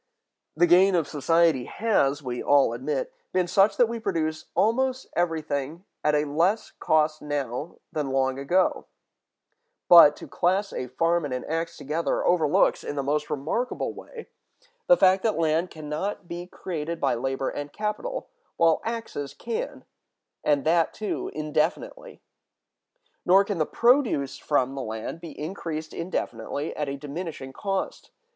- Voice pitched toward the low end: No, medium, 160 Hz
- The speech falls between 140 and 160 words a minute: Yes, average, 150 wpm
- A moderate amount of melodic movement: Yes, average, 4.6 semitones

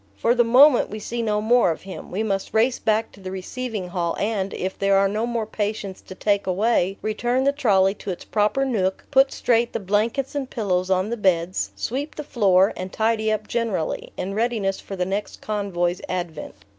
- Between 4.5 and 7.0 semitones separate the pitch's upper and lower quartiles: No, average, 3.6 semitones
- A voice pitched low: No, high, 210 Hz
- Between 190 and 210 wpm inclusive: Yes, fast, 205 wpm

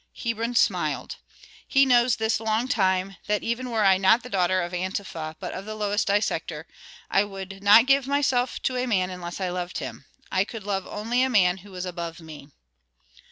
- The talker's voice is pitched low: No, high, 200 Hz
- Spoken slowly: No, average, 195 wpm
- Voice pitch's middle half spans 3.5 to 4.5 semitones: Yes, average, 4.0 semitones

